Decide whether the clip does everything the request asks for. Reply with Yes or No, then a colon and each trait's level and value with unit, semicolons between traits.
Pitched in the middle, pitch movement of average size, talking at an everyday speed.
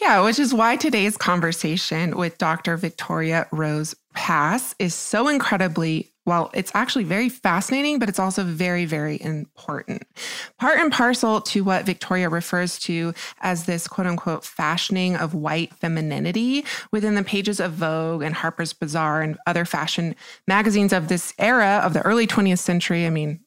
Yes: medium, 180 Hz; average, 4.1 semitones; average, 160 wpm